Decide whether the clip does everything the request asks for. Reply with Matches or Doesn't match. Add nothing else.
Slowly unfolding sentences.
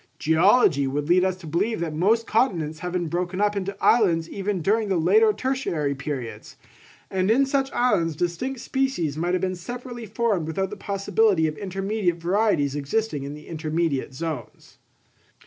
Doesn't match